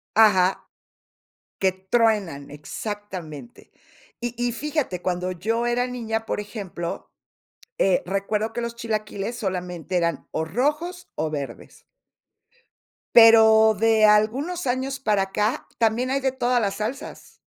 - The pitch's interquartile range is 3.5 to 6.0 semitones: Yes, average, 4.2 semitones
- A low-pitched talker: No, high, 220 Hz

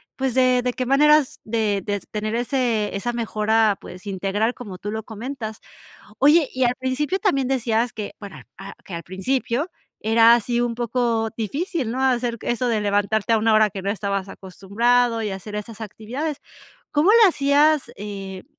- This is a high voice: Yes, high, 230 Hz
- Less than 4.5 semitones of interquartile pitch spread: Yes, average, 3.7 semitones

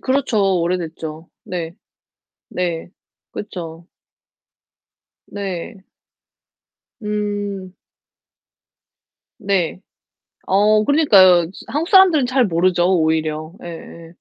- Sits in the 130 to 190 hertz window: Yes, medium, 185 Hz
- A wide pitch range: No, average, 3.9 semitones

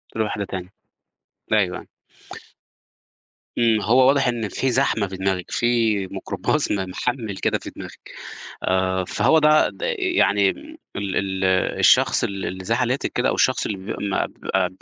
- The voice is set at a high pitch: No, low, 105 Hz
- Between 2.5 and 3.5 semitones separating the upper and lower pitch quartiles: No, average, 4.2 semitones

